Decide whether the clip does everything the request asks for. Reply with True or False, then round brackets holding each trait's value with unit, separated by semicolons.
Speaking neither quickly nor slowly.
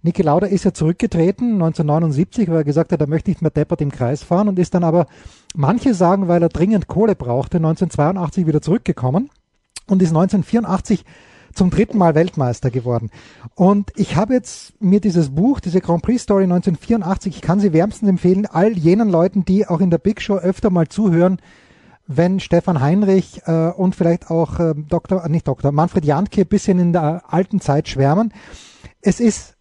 True (180 wpm)